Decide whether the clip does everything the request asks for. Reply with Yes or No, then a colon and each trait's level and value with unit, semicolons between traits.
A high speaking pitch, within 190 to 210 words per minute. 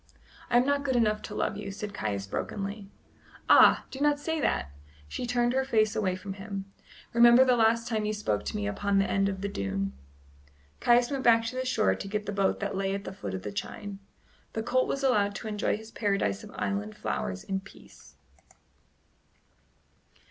Yes: high, 205 Hz; average, 200 wpm